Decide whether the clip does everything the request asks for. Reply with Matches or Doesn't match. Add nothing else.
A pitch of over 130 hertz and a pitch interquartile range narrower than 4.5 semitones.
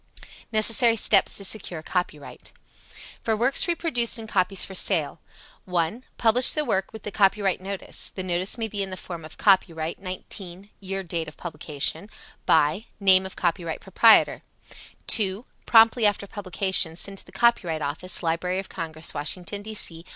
Matches